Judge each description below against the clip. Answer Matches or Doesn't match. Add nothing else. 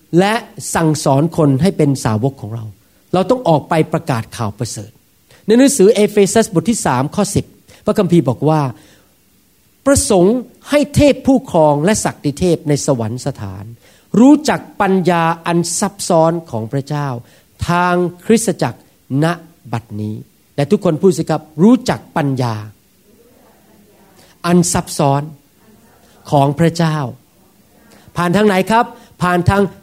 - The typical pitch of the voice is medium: Matches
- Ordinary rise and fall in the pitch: Doesn't match